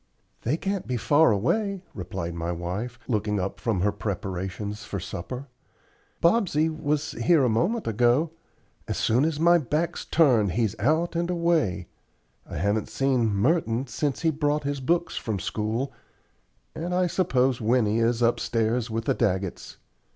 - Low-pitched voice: Yes, low, 125 Hz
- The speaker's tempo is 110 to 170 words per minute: Yes, average, 150 wpm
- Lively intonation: Yes, wide, 7.1 semitones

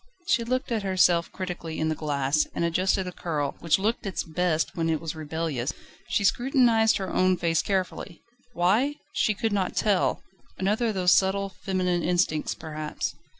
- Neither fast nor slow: Yes, average, 170 wpm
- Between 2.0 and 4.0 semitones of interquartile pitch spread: Yes, average, 3.7 semitones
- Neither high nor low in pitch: Yes, medium, 180 Hz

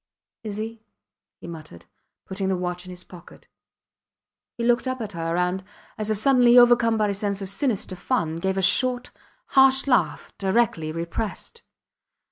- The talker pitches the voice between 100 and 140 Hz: No, high, 200 Hz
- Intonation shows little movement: No, average, 5.1 semitones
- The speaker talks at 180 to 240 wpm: No, average, 160 wpm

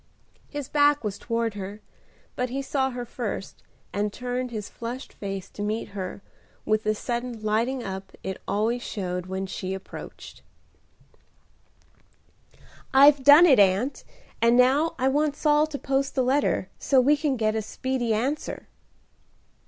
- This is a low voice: No, high, 240 Hz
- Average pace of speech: Yes, average, 150 wpm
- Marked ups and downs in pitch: No, average, 4.5 semitones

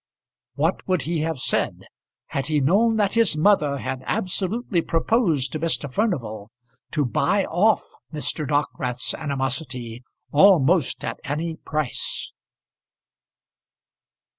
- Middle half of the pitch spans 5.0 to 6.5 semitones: Yes, wide, 5.5 semitones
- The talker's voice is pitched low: No, medium, 155 Hz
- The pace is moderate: No, slow, 115 wpm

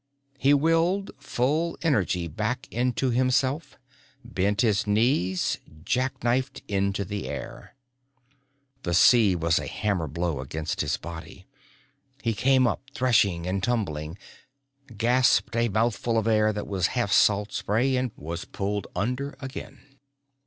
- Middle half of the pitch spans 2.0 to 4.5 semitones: No, average, 5.1 semitones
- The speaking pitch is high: No, low, 110 Hz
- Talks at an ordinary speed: No, slow, 130 wpm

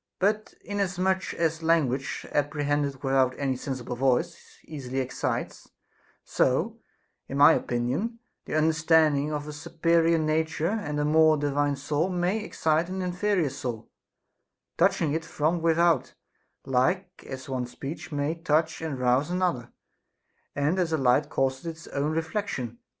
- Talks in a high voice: No, medium, 155 Hz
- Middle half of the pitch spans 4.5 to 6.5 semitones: No, average, 3.5 semitones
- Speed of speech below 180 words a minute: Yes, average, 140 wpm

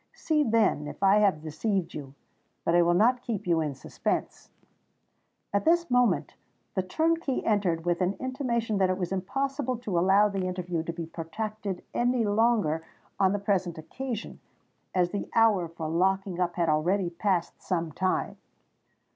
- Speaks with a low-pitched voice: No, high, 190 Hz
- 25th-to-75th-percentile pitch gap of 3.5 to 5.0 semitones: Yes, average, 4.7 semitones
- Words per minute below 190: Yes, average, 160 wpm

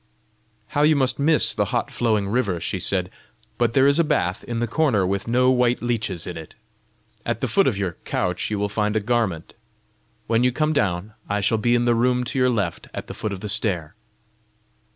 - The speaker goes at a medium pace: No, fast, 215 wpm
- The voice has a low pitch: Yes, low, 115 Hz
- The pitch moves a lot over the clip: No, average, 4.0 semitones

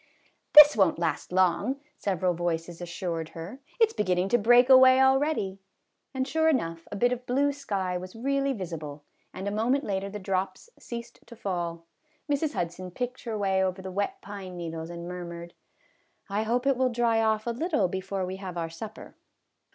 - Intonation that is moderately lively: No, wide, 5.9 semitones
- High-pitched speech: Yes, high, 200 Hz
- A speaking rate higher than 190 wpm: Yes, average, 200 wpm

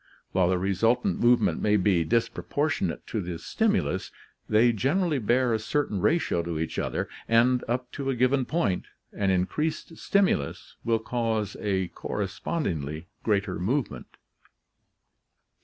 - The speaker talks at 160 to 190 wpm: No, slow, 135 wpm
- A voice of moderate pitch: No, low, 110 Hz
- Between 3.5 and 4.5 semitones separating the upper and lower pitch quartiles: No, wide, 5.4 semitones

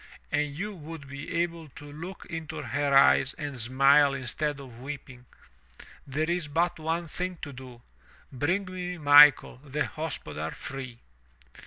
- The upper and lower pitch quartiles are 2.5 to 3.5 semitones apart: Yes, average, 3.1 semitones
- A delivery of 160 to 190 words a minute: No, average, 150 wpm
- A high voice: No, medium, 145 Hz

